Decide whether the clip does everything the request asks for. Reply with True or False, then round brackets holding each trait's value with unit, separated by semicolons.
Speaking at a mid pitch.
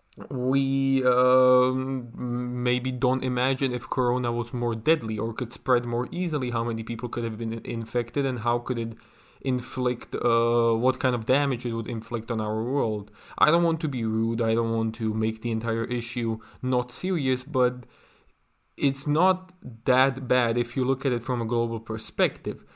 False (125 Hz)